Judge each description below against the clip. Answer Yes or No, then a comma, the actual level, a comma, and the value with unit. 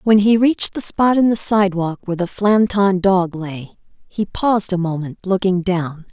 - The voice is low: No, high, 190 Hz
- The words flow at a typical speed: Yes, average, 185 wpm